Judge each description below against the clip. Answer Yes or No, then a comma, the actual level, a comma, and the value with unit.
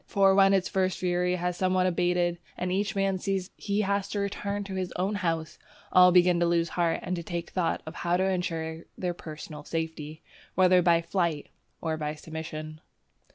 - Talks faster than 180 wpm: Yes, average, 190 wpm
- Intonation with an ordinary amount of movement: No, narrow, 2.3 semitones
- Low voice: No, medium, 180 Hz